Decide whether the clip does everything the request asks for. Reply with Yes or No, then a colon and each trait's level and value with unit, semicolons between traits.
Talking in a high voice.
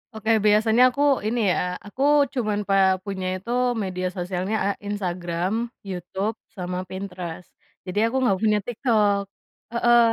Yes: high, 200 Hz